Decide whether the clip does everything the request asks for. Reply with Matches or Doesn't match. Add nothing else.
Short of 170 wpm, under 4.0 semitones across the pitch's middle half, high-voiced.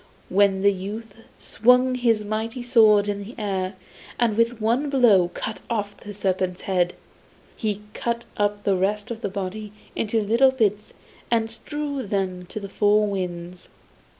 Matches